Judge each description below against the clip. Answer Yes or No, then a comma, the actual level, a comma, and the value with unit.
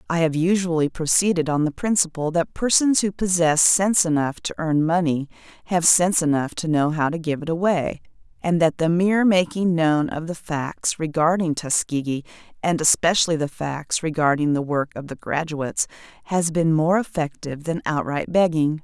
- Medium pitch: Yes, medium, 165 Hz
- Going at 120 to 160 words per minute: No, average, 170 wpm